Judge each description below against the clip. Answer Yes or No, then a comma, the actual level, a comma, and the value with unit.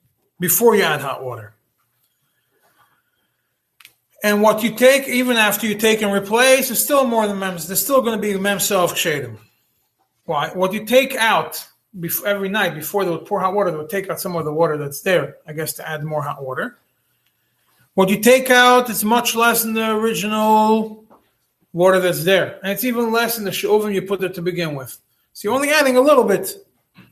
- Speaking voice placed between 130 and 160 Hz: No, high, 200 Hz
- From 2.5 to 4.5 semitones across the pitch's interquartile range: No, average, 4.9 semitones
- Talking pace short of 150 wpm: No, average, 200 wpm